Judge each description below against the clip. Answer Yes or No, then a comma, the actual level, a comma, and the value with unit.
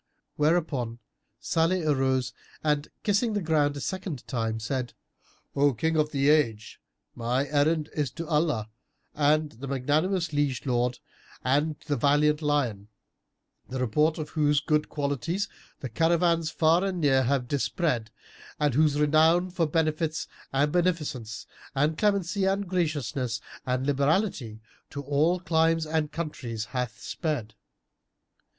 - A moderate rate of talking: No, slow, 130 wpm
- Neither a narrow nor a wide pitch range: Yes, average, 3.7 semitones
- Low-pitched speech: No, medium, 150 Hz